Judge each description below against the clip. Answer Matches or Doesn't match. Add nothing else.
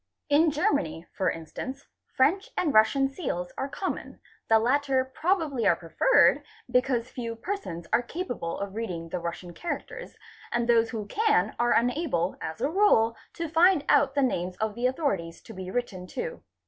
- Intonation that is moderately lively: Doesn't match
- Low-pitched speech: Doesn't match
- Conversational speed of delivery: Matches